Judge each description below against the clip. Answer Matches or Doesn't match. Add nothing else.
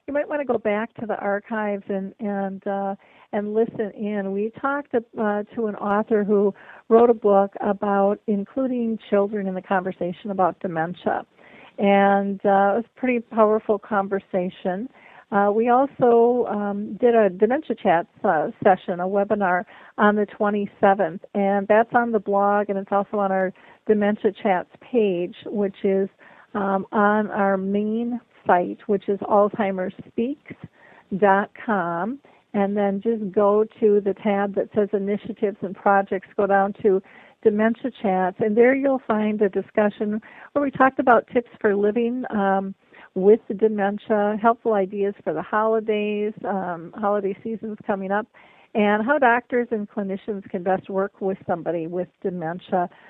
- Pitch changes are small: Matches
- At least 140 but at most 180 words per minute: Matches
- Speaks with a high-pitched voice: Matches